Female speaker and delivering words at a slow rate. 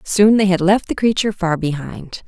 No: female; fast, 210 wpm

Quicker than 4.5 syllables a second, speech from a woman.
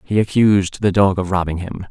No: 5.6 syllables/s; male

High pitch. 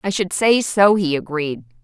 No: medium, 180 Hz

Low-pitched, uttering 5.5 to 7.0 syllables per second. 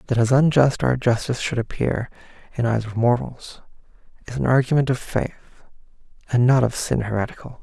Yes: low, 125 Hz; 5.8 syllables/s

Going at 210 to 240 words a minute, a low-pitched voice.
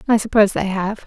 No: fast, 225 wpm; high, 205 Hz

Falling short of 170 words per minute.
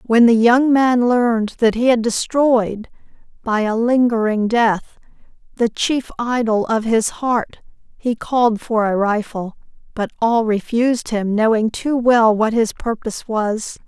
Yes: average, 150 wpm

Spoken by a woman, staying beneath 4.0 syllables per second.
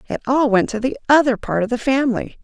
No: female; 6.3 syllables/s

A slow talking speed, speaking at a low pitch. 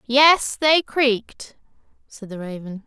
No: slow, 125 wpm; high, 245 Hz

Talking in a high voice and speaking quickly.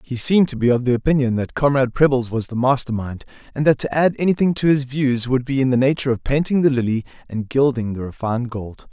No: low, 130 Hz; fast, 240 wpm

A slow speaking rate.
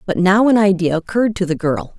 No: fast, 240 wpm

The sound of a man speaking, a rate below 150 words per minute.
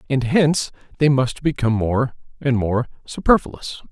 Yes: male; average, 140 wpm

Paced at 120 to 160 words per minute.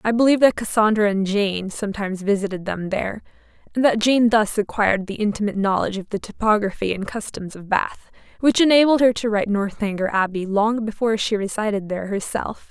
No: average, 180 wpm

